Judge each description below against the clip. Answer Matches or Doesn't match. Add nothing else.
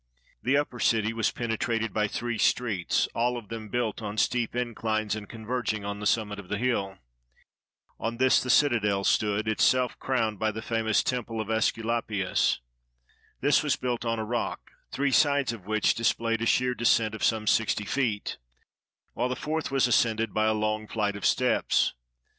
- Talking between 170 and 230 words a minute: Matches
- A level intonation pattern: Matches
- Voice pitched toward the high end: Doesn't match